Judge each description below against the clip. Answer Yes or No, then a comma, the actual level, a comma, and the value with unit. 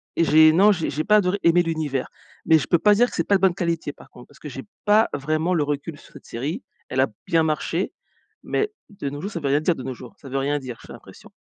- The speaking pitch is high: No, medium, 160 Hz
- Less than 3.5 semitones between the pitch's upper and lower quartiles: No, average, 4.3 semitones